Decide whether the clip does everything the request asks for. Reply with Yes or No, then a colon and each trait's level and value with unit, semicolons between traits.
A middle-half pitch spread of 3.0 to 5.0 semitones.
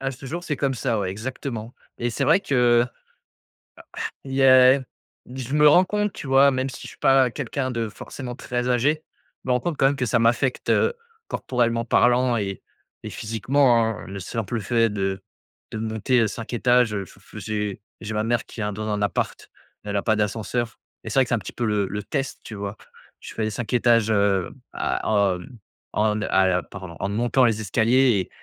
Yes: average, 3.7 semitones